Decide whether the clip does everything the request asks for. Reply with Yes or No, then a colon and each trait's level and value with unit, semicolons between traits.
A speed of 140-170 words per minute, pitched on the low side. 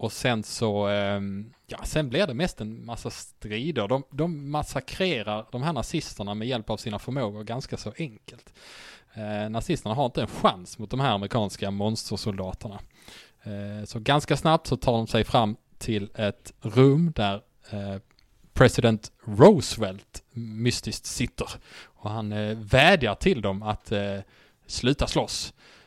Yes: average, 150 wpm; low, 110 Hz